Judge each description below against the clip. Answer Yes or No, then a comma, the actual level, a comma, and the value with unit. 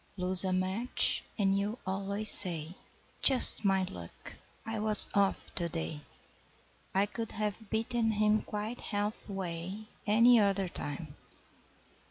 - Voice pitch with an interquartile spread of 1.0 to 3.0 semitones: Yes, average, 2.7 semitones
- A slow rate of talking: Yes, slow, 130 wpm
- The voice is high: Yes, high, 200 Hz